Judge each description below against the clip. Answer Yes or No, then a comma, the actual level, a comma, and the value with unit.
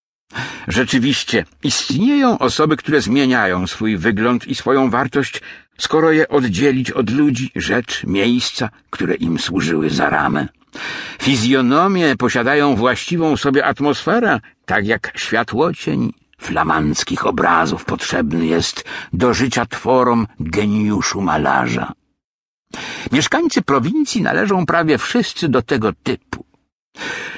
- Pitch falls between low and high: No, low, 130 Hz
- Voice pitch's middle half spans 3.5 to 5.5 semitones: Yes, average, 5.1 semitones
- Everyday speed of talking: No, slow, 105 wpm